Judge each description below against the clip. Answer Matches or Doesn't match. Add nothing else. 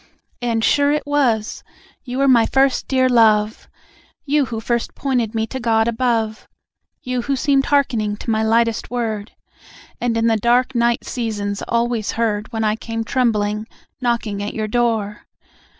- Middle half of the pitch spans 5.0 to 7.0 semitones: Doesn't match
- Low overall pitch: Doesn't match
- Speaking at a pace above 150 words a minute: Matches